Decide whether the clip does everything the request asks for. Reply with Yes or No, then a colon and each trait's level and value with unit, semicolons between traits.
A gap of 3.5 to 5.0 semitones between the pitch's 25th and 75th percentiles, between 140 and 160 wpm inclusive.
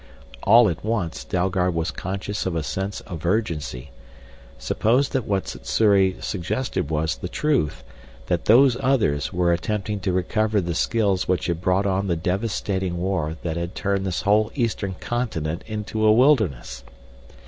Yes: average, 4.0 semitones; average, 155 wpm